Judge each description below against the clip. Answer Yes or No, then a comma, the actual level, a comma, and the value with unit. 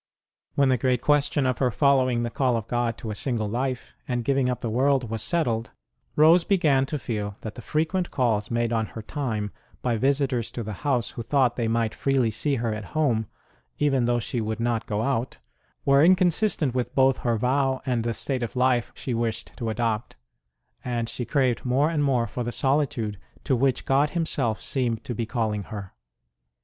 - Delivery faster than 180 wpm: Yes, average, 200 wpm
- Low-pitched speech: Yes, low, 125 Hz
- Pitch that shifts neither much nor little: Yes, average, 3.2 semitones